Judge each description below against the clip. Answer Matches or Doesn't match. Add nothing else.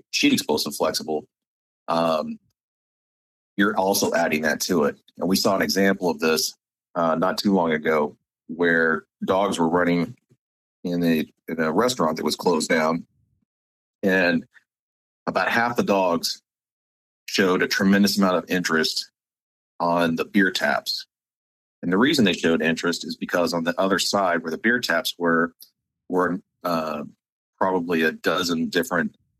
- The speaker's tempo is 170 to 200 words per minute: Doesn't match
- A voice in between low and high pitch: Doesn't match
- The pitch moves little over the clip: Doesn't match